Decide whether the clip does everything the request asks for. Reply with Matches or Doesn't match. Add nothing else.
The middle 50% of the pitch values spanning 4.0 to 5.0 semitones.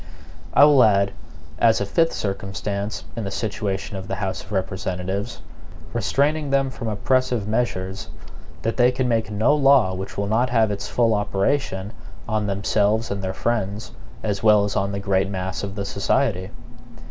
Doesn't match